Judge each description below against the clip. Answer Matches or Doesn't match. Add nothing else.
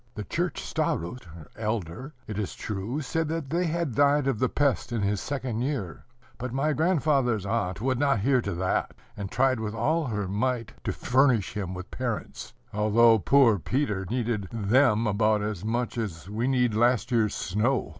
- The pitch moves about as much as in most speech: Matches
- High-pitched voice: Doesn't match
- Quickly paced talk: Doesn't match